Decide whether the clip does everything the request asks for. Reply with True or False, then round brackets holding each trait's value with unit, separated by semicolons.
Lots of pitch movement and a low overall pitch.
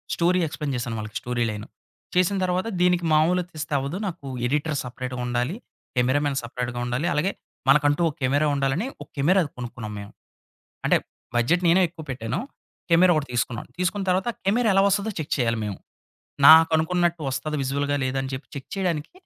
False (5.9 semitones; 150 Hz)